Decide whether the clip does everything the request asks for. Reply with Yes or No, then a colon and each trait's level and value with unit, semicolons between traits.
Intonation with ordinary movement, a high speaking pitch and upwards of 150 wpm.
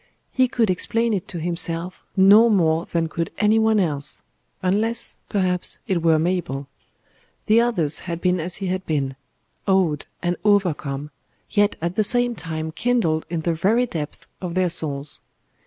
No: average, 4.5 semitones; medium, 180 Hz; average, 160 wpm